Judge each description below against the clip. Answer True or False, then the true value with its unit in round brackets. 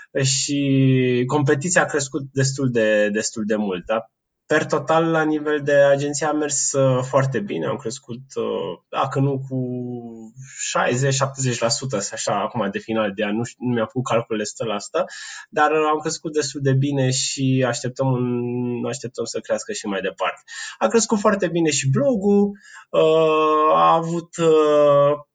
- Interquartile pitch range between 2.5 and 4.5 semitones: True (3.7 semitones)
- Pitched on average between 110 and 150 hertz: True (135 Hz)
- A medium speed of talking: True (150 wpm)